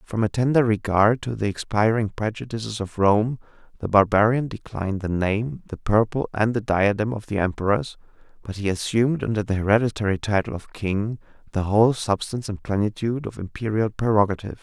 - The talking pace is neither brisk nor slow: Yes, average, 165 wpm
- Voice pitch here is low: Yes, low, 110 Hz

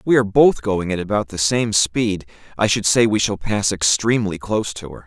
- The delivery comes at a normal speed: No, fast, 235 wpm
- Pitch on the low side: Yes, low, 105 Hz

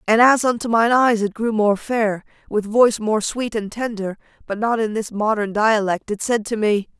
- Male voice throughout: No, female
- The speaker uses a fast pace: Yes, fast, 215 wpm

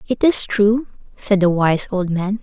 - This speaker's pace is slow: No, average, 200 wpm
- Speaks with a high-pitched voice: Yes, high, 200 Hz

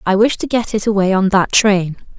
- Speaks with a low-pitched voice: No, high, 200 Hz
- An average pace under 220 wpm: No, fast, 245 wpm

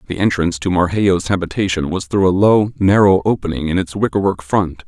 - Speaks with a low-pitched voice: Yes, very low, 90 Hz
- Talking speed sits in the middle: Yes, average, 195 wpm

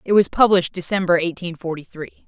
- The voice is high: No, medium, 175 Hz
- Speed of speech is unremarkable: Yes, average, 185 wpm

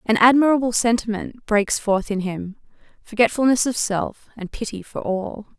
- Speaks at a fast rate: No, average, 150 wpm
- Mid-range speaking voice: No, high, 220 Hz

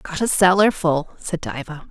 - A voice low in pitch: No, medium, 170 Hz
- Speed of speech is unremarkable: Yes, average, 190 wpm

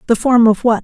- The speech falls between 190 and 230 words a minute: No, fast, 290 wpm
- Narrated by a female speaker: Yes, female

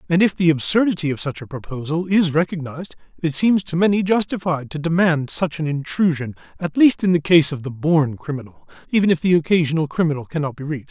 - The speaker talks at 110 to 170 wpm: No, fast, 205 wpm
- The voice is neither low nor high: Yes, medium, 160 Hz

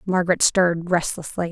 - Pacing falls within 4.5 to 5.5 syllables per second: No, 5.8 syllables/s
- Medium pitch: Yes, medium, 175 Hz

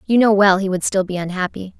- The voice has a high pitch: Yes, high, 195 Hz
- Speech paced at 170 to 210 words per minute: No, fast, 265 wpm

